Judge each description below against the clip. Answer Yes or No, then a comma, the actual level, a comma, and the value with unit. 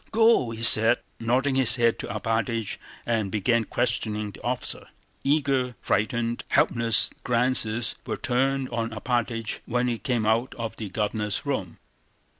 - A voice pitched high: No, low, 115 Hz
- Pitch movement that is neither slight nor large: No, narrow, 2.1 semitones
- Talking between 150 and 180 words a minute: No, average, 140 wpm